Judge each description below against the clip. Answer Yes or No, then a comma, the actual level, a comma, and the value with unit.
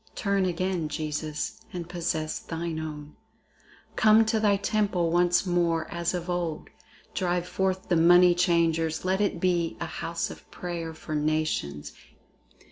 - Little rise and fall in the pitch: Yes, narrow, 2.2 semitones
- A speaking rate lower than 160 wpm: Yes, average, 140 wpm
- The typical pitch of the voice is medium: Yes, medium, 175 Hz